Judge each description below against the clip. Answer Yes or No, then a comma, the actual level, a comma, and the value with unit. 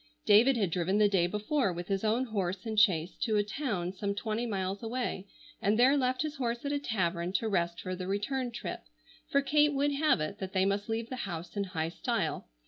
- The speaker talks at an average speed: No, fast, 220 wpm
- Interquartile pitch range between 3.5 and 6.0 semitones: Yes, average, 5.1 semitones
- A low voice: No, high, 210 Hz